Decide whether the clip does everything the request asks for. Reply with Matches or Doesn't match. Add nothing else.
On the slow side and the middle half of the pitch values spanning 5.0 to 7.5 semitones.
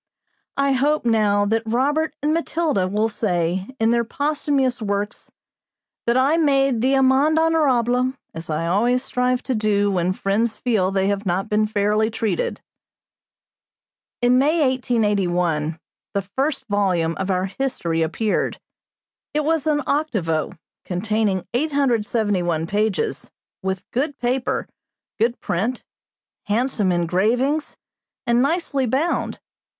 Matches